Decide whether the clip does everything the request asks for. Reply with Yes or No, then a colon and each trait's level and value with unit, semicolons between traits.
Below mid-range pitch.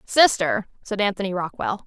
No: high, 195 Hz